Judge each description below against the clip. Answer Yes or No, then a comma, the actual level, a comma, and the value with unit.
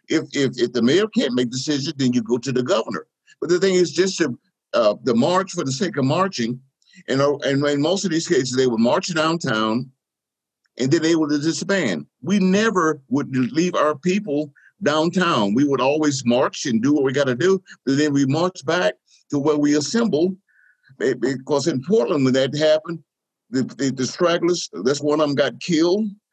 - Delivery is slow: No, average, 195 wpm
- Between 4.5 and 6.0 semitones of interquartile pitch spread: Yes, wide, 5.4 semitones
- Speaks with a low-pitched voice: No, medium, 155 Hz